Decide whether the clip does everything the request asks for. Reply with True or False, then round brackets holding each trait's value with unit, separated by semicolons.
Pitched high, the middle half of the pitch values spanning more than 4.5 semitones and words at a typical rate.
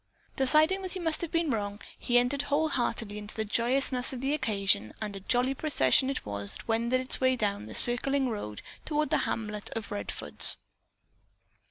True (245 Hz; 5.0 semitones; 180 wpm)